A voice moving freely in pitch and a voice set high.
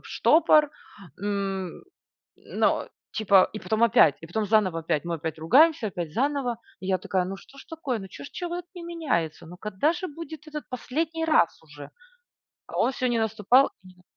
Yes: wide, 8.4 semitones; high, 220 Hz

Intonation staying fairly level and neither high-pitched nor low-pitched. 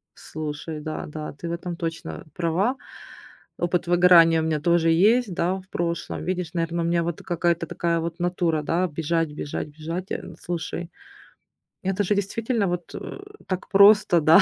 Yes: narrow, 1.9 semitones; medium, 170 Hz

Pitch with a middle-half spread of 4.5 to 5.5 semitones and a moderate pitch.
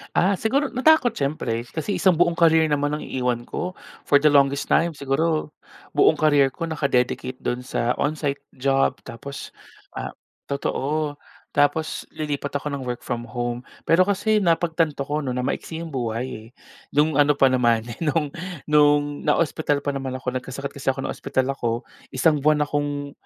No: average, 3.2 semitones; medium, 145 Hz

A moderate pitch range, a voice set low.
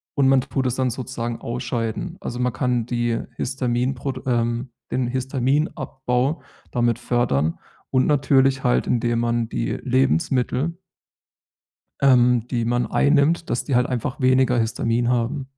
No: narrow, 1.9 semitones; low, 125 Hz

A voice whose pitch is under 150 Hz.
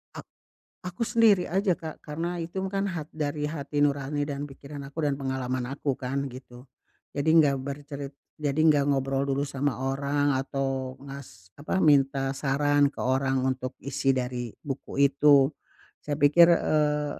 Yes: medium, 140 Hz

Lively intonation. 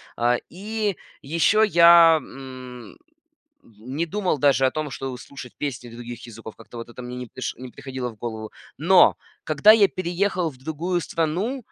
Yes: wide, 5.9 semitones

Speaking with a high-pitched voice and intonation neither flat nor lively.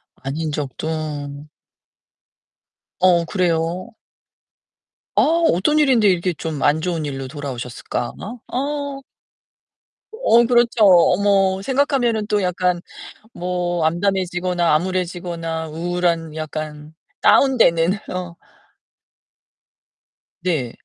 No: medium, 175 Hz; average, 4.0 semitones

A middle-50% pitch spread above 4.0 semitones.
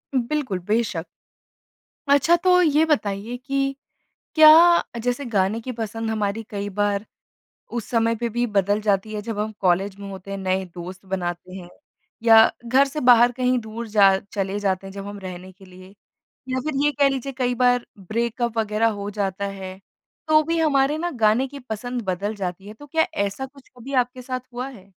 Yes: average, 4.4 semitones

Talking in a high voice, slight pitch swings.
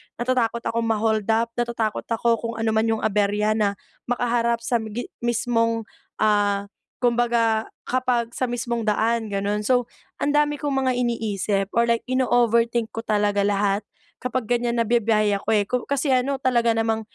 Yes: high, 230 Hz; narrow, 1.9 semitones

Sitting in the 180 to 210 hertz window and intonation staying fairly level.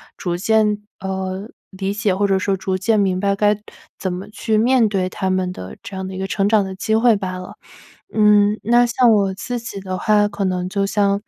Yes: high, 200 Hz; narrow, 2.1 semitones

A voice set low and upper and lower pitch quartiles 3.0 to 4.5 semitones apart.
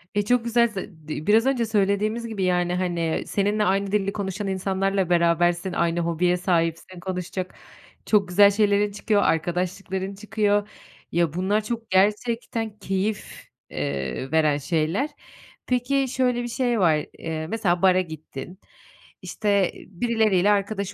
No: high, 195 Hz; average, 3.5 semitones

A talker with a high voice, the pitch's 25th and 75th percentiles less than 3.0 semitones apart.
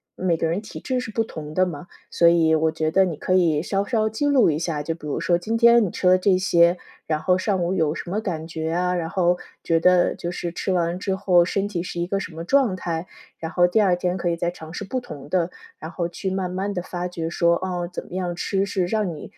No: medium, 180 Hz; narrow, 2.4 semitones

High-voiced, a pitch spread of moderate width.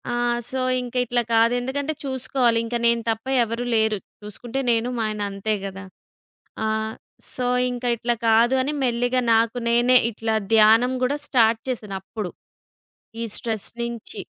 No: high, 235 Hz; narrow, 2.0 semitones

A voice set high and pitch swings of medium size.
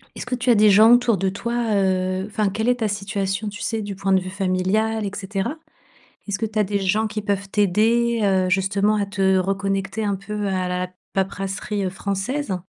No: high, 200 Hz; narrow, 2.0 semitones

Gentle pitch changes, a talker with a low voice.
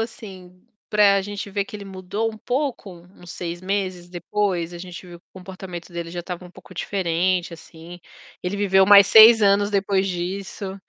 No: narrow, 2.3 semitones; high, 190 Hz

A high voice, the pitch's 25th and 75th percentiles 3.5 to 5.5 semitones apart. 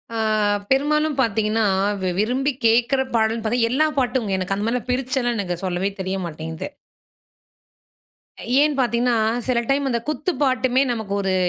Yes: high, 240 Hz; average, 3.9 semitones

